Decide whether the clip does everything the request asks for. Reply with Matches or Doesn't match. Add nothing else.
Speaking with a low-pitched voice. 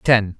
Matches